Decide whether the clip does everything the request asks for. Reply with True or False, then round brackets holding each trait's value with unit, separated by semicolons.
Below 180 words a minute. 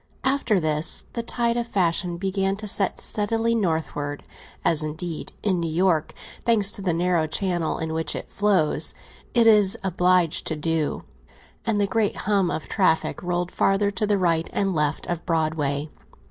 True (165 wpm)